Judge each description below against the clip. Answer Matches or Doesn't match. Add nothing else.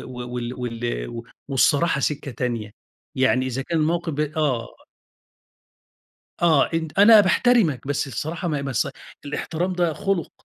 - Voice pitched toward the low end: Doesn't match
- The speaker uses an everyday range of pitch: Matches